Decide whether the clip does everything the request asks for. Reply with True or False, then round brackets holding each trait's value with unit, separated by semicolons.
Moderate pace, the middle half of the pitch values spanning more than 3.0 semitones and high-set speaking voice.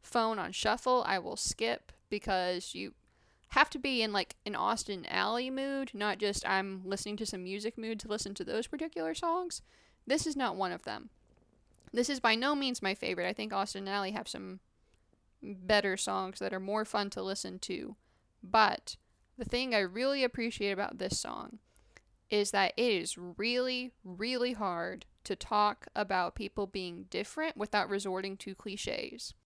True (175 wpm; 4.0 semitones; 210 Hz)